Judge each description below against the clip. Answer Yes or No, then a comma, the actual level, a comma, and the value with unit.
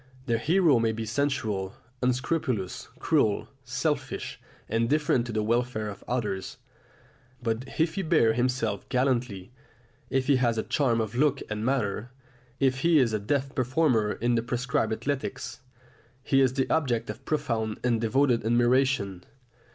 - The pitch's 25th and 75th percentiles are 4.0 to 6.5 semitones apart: No, average, 3.4 semitones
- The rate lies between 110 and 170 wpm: Yes, average, 145 wpm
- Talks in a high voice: No, low, 125 Hz